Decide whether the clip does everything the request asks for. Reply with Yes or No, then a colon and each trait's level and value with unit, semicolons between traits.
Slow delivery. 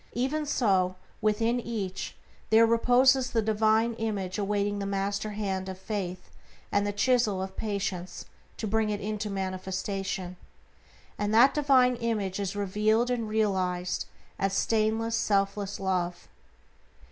Yes: slow, 130 wpm